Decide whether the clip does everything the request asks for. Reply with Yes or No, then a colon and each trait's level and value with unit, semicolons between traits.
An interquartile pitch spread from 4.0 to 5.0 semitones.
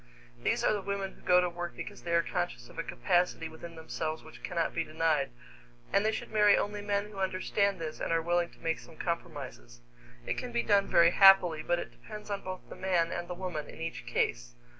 No: average, 3.3 semitones